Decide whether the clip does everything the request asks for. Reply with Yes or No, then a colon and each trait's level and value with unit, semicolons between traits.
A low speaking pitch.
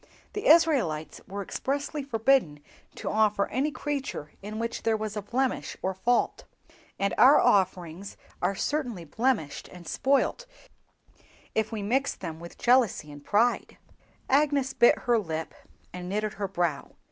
No: high, 220 Hz